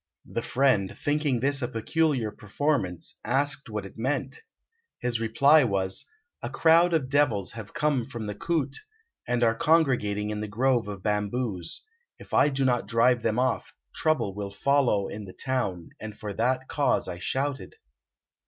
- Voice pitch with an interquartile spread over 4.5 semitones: Yes, average, 5.0 semitones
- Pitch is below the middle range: Yes, low, 120 Hz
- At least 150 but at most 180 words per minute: Yes, average, 160 wpm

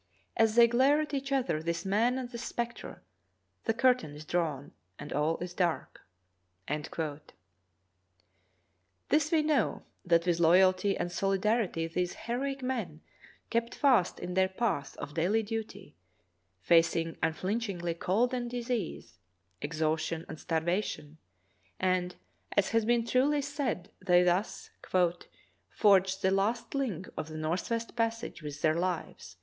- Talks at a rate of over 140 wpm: No, slow, 135 wpm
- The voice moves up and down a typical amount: No, wide, 6.5 semitones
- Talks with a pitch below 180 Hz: No, medium, 185 Hz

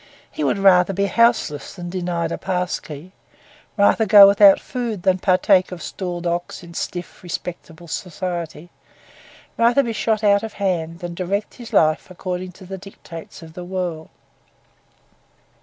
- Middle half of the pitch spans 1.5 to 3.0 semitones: Yes, narrow, 2.5 semitones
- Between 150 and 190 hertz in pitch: Yes, medium, 185 Hz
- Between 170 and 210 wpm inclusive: No, average, 155 wpm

